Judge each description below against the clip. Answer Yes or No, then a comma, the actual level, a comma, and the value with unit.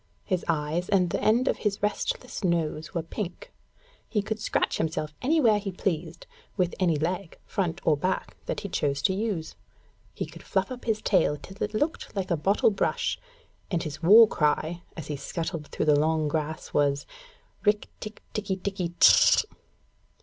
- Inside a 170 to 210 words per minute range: Yes, average, 175 wpm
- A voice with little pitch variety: No, average, 4.8 semitones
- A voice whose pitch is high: No, medium, 180 Hz